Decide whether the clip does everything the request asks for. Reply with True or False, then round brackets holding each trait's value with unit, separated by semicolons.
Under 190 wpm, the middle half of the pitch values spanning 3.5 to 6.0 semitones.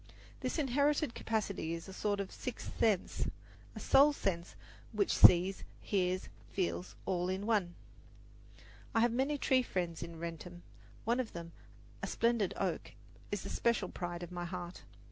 True (155 wpm; 4.9 semitones)